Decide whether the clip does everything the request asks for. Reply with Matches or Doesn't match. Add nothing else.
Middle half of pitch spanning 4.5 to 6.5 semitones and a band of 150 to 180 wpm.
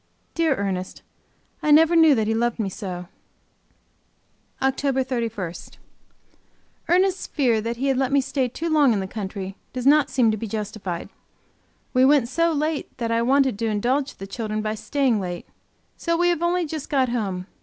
Matches